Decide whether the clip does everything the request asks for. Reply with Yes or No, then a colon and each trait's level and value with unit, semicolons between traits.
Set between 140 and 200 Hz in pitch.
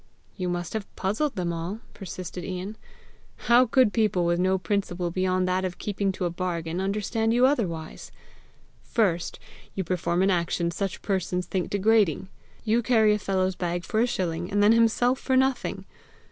Yes: high, 190 Hz